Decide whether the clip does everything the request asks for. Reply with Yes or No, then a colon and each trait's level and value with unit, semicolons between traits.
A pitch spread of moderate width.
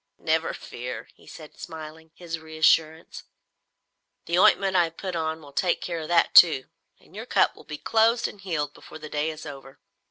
No: narrow, 2.2 semitones